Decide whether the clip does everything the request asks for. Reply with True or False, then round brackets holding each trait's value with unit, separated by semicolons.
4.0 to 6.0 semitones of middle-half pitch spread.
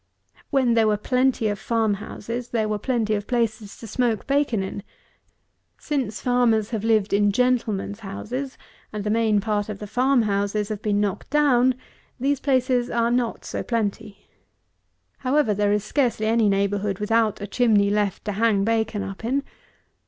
False (3.1 semitones)